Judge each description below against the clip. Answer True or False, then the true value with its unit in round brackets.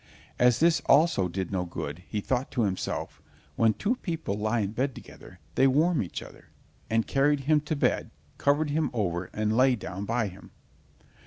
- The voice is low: True (120 Hz)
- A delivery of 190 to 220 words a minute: False (180 wpm)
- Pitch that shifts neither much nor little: False (6.4 semitones)